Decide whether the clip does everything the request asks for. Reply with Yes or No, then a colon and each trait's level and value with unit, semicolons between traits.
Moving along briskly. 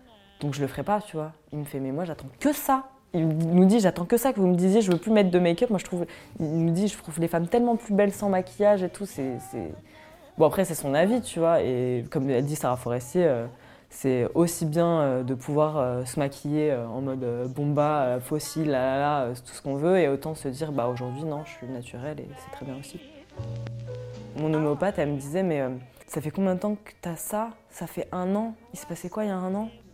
Yes: fast, 250 wpm